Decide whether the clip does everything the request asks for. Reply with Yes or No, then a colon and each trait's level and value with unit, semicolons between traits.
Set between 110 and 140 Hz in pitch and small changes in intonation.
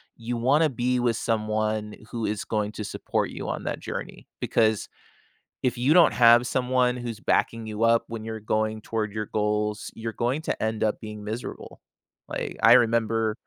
Yes: low, 115 Hz; narrow, 2.0 semitones